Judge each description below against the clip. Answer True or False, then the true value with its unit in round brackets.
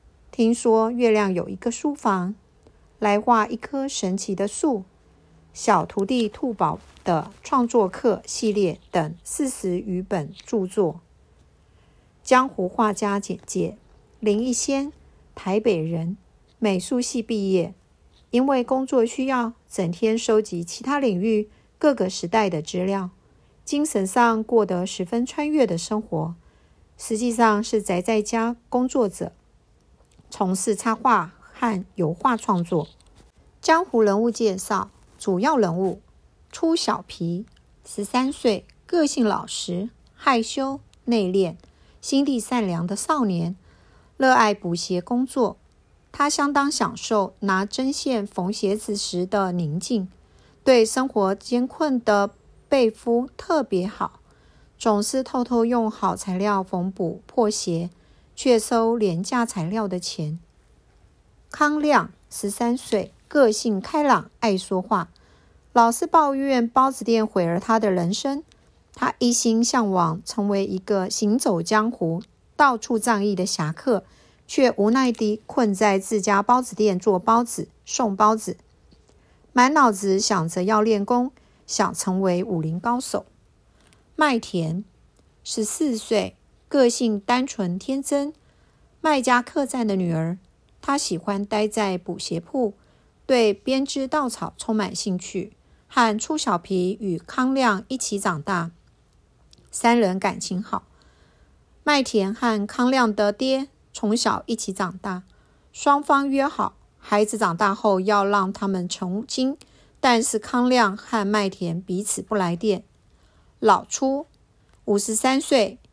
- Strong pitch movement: False (4.5 semitones)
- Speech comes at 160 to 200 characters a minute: True (190 characters per minute)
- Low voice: False (220 Hz)